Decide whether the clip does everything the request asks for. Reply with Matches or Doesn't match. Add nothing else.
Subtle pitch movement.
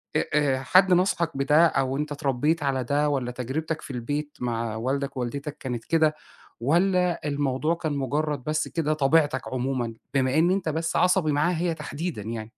Doesn't match